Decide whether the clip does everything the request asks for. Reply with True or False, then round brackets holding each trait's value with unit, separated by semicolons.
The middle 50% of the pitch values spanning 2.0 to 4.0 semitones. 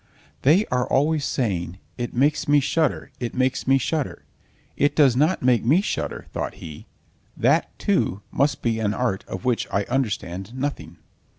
False (4.5 semitones)